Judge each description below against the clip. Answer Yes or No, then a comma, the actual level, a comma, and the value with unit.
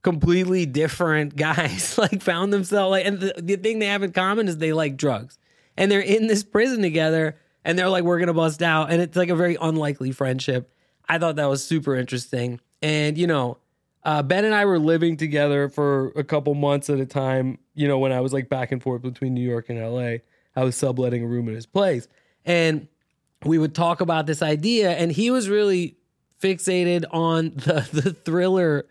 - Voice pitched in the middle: Yes, medium, 160 Hz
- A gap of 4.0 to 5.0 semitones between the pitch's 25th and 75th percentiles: Yes, average, 4.5 semitones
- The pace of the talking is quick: Yes, fast, 210 wpm